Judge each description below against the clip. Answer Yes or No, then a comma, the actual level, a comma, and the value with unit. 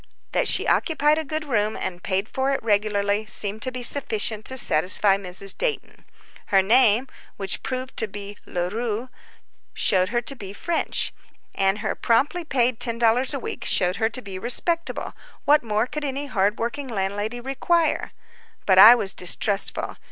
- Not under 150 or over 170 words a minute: Yes, average, 160 wpm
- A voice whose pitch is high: Yes, high, 225 Hz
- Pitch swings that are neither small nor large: Yes, average, 4.6 semitones